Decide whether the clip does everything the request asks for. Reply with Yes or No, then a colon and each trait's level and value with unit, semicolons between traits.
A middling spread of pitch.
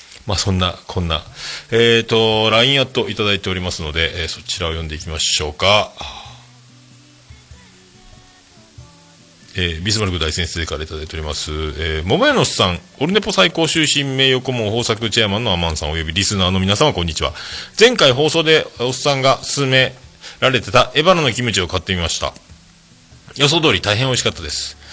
No: wide, 7.4 semitones